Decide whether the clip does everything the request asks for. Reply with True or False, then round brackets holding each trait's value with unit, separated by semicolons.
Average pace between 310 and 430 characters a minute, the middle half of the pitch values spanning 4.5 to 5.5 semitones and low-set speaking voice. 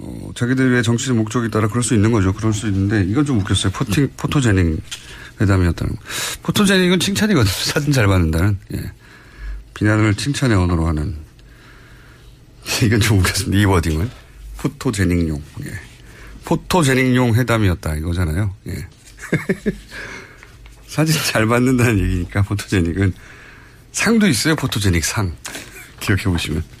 True (315 characters per minute; 5.1 semitones; 110 Hz)